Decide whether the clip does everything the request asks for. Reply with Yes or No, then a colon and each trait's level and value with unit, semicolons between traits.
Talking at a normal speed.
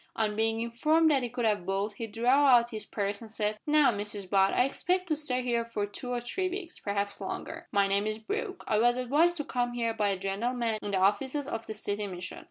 No: fast, 240 wpm